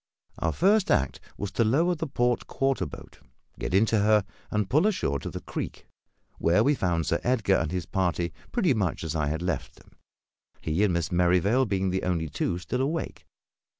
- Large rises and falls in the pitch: Yes, wide, 6.8 semitones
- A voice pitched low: Yes, very low, 95 Hz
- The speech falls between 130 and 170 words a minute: No, average, 190 wpm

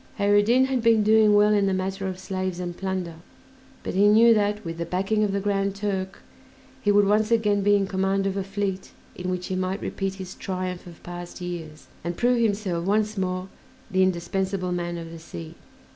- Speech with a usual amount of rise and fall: No, narrow, 2.1 semitones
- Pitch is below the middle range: No, high, 195 Hz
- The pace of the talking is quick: Yes, fast, 210 wpm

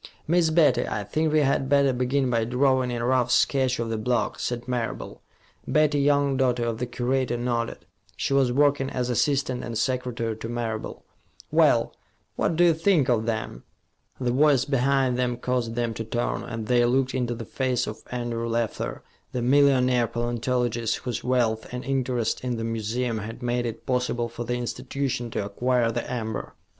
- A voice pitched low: Yes, low, 125 Hz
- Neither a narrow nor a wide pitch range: No, narrow, 2.1 semitones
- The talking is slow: No, average, 175 wpm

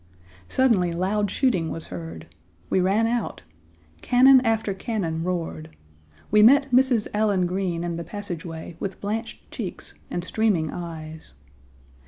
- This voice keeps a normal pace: No, slow, 130 wpm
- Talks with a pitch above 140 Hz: Yes, high, 190 Hz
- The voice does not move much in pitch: No, average, 4.9 semitones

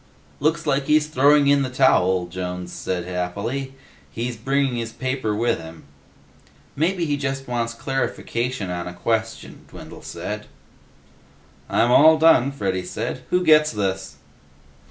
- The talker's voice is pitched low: Yes, low, 125 Hz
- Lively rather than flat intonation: Yes, wide, 6.5 semitones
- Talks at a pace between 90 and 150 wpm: Yes, slow, 135 wpm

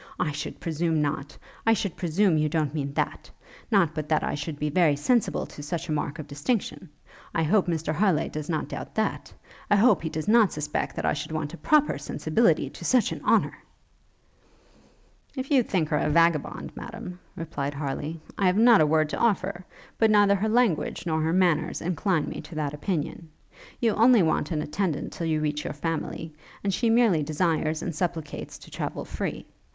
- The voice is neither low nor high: Yes, medium, 165 Hz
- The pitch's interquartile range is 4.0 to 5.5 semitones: Yes, average, 4.6 semitones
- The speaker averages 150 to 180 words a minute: No, average, 195 wpm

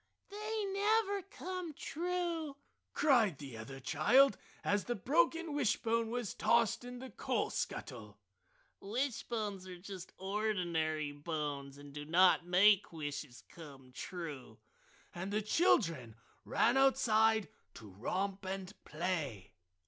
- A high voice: Yes, high, 195 Hz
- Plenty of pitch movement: Yes, wide, 8.6 semitones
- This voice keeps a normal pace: No, slow, 120 wpm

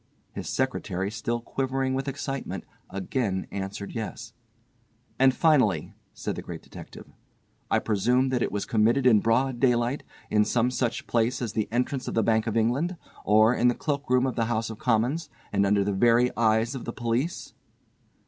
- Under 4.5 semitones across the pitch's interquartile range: Yes, average, 3.0 semitones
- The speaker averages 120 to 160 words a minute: No, average, 175 wpm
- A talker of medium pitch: No, low, 120 Hz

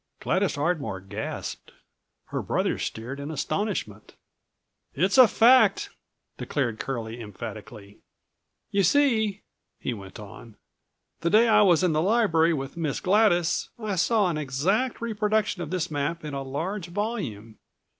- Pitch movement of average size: No, wide, 7.8 semitones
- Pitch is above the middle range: No, medium, 165 Hz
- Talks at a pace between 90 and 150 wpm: Yes, slow, 135 wpm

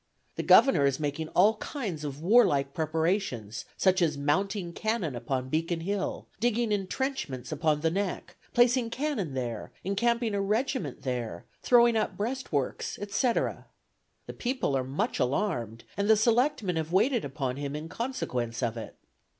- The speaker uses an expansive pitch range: Yes, wide, 8.0 semitones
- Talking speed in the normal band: Yes, average, 150 wpm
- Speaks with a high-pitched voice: No, medium, 175 Hz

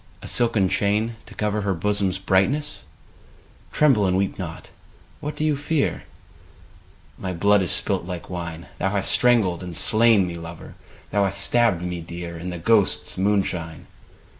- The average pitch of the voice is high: No, very low, 95 Hz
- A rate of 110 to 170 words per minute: Yes, average, 165 wpm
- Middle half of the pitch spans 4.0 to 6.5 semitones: No, average, 3.5 semitones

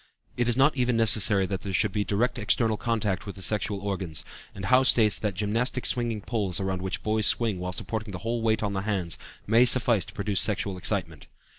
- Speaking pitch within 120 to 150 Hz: No, low, 105 Hz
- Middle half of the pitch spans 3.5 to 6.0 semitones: No, average, 3.0 semitones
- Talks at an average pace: No, fast, 210 wpm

